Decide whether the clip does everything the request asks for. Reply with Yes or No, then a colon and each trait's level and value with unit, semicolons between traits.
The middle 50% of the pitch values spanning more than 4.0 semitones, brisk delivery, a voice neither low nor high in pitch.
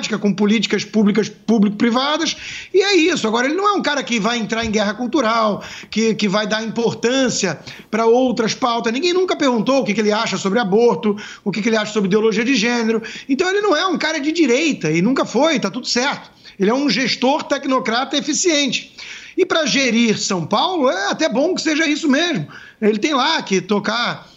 No: average, 5.3 semitones; fast, 205 wpm; high, 235 Hz